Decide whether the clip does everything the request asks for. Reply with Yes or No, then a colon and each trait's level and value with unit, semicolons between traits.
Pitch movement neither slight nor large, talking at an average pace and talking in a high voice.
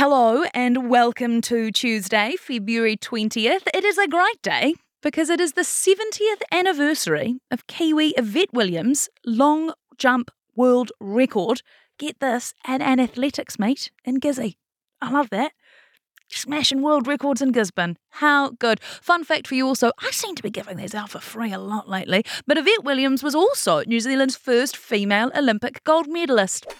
Yes: average, 4.5 semitones; average, 165 wpm; very high, 260 Hz